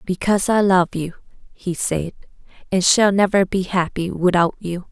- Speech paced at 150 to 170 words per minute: Yes, average, 160 wpm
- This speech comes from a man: No, female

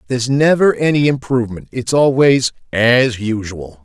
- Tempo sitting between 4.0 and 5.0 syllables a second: Yes, 4.7 syllables/s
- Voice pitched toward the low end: Yes, low, 125 Hz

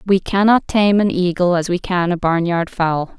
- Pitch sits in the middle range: Yes, medium, 180 Hz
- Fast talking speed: Yes, fast, 225 wpm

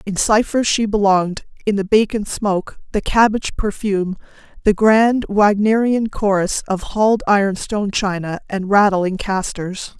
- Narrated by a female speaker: Yes, female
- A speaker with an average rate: No, slow, 125 wpm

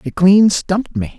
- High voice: No, medium, 175 Hz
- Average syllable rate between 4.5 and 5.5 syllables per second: Yes, 4.7 syllables/s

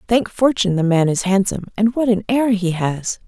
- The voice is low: No, high, 205 Hz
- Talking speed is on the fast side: Yes, fast, 220 wpm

